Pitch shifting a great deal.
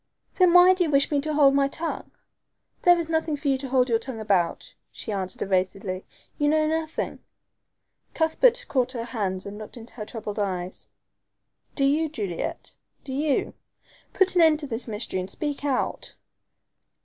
Yes: wide, 6.7 semitones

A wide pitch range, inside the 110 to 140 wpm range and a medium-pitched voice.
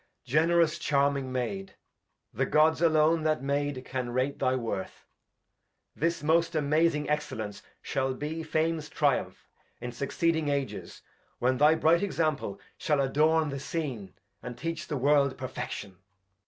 No: average, 3.6 semitones; slow, 135 wpm; medium, 150 Hz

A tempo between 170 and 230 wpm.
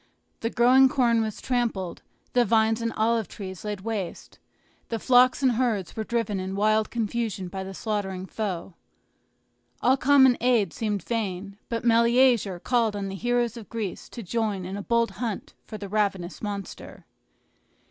No: average, 160 wpm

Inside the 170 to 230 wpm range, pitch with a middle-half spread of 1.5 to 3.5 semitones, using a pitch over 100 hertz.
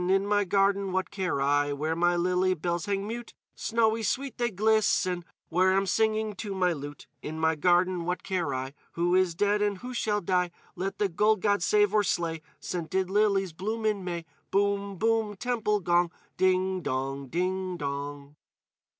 Yes: average, 175 wpm; average, 3.2 semitones; medium, 185 Hz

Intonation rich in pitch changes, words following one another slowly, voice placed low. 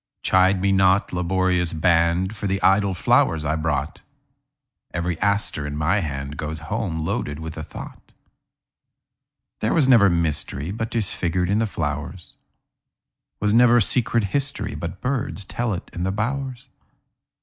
No: average, 4.3 semitones; slow, 125 wpm; very low, 95 Hz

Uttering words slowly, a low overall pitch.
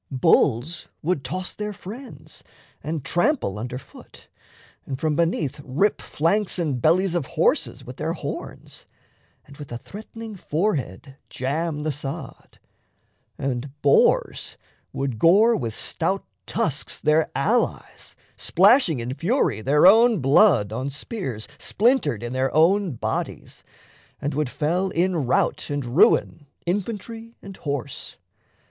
No: slow, 130 wpm; medium, 155 Hz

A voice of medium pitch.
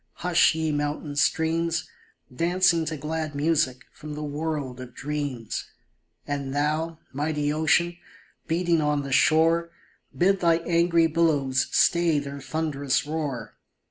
Yes: medium, 155 Hz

